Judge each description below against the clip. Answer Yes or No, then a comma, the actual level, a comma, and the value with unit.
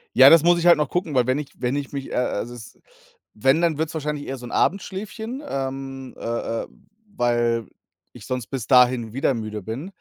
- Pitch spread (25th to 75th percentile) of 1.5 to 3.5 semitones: No, average, 4.3 semitones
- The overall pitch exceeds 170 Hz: No, low, 135 Hz